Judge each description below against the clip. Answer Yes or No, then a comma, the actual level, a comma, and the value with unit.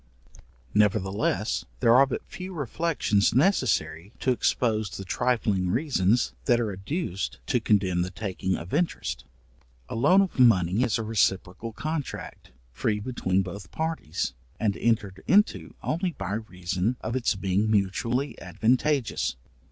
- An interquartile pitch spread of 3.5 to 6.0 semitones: Yes, average, 5.1 semitones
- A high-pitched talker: No, low, 110 Hz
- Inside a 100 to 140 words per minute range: Yes, slow, 135 wpm